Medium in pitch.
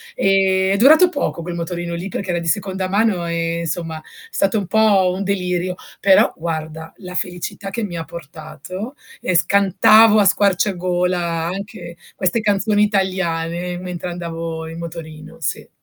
Yes: medium, 180 Hz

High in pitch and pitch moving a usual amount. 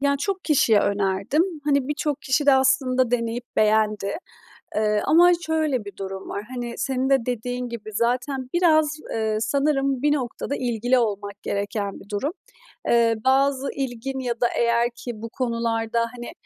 Yes: high, 245 Hz; average, 3.7 semitones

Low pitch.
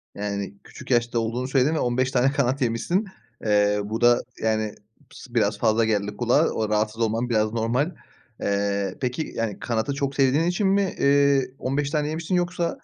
Yes: low, 120 Hz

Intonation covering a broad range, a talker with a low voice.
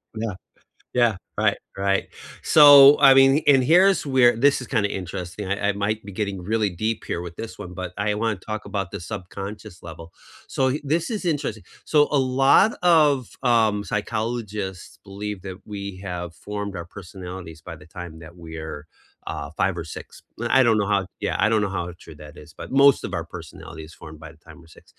Yes: wide, 5.7 semitones; low, 105 Hz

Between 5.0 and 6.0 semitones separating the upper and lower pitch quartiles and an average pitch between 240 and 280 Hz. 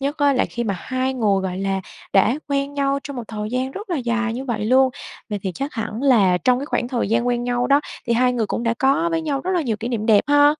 No: average, 3.8 semitones; high, 245 Hz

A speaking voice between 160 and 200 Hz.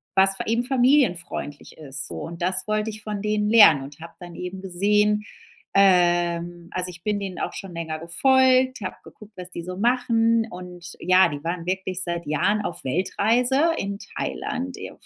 Yes: high, 190 Hz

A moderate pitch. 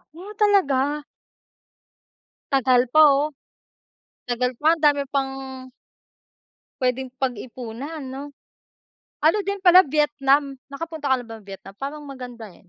No: very high, 275 Hz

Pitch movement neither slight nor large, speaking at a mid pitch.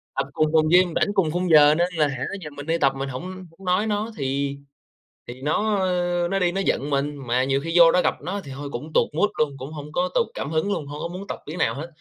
Yes: average, 4.3 semitones; medium, 160 Hz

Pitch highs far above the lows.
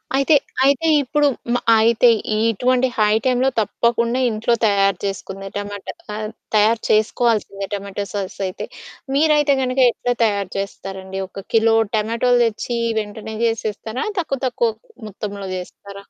No: average, 3.5 semitones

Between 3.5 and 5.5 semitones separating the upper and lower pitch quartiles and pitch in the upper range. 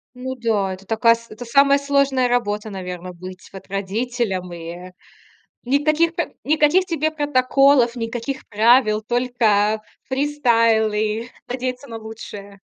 Yes: average, 4.2 semitones; high, 235 Hz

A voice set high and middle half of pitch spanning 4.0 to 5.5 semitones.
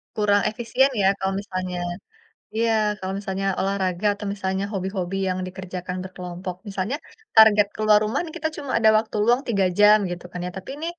No: high, 195 Hz; narrow, 2.6 semitones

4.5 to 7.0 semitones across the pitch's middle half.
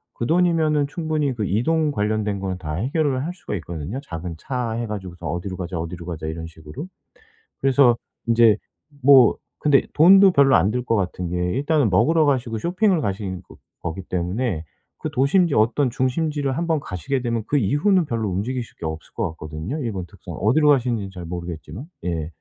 No: wide, 8.0 semitones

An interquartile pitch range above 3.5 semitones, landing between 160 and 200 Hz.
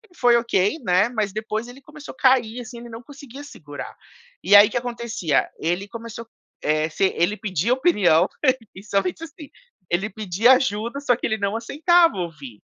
No: average, 4.8 semitones; high, 225 Hz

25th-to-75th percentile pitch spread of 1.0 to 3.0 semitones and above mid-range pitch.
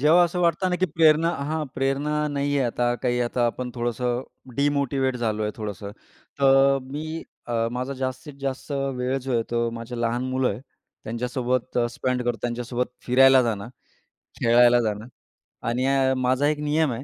No: average, 2.7 semitones; low, 130 Hz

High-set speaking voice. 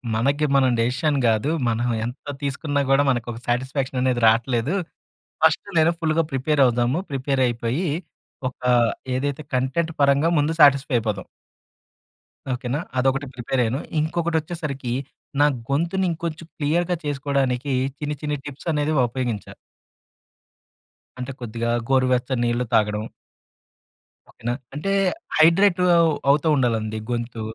No: low, 135 Hz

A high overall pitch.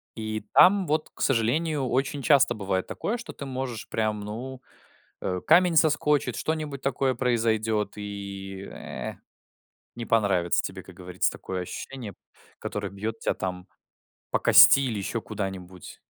No: low, 115 Hz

